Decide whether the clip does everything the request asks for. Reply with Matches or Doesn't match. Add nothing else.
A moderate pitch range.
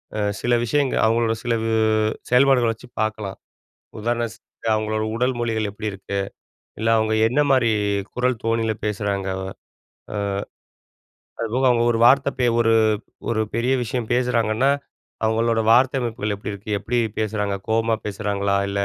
Doesn't match